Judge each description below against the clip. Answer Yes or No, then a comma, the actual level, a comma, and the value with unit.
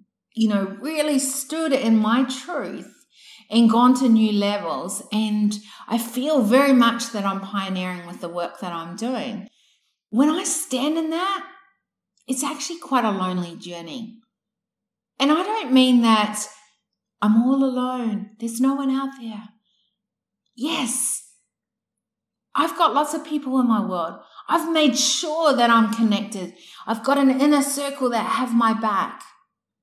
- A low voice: No, high, 230 Hz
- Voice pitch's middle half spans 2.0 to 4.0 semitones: No, average, 4.7 semitones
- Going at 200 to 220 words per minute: No, average, 150 wpm